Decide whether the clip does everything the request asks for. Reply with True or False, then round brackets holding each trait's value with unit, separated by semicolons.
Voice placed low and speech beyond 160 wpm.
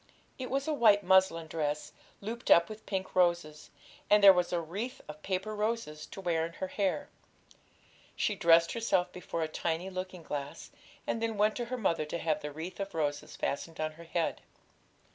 False (180 Hz; 190 wpm)